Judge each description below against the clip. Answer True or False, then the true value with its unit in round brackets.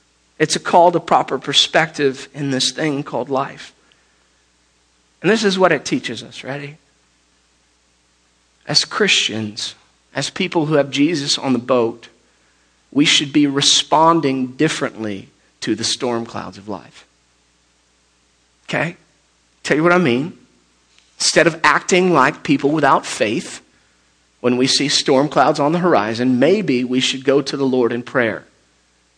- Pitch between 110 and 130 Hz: True (125 Hz)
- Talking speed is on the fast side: False (145 wpm)